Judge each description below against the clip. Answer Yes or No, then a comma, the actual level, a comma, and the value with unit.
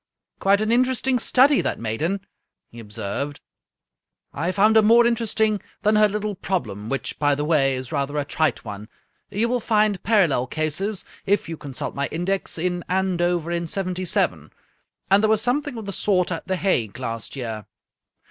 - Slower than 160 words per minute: No, average, 175 wpm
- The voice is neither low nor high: Yes, medium, 180 Hz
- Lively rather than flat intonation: Yes, wide, 7.0 semitones